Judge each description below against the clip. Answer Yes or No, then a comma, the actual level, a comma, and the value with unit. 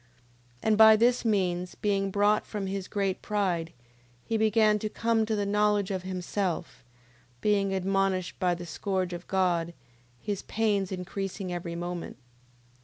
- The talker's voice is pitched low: No, high, 195 Hz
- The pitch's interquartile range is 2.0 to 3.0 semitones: Yes, narrow, 2.5 semitones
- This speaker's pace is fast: No, average, 150 wpm